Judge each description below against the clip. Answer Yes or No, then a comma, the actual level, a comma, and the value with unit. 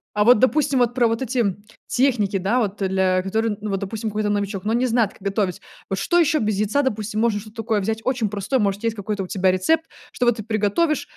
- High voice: Yes, high, 215 Hz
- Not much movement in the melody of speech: No, average, 3.2 semitones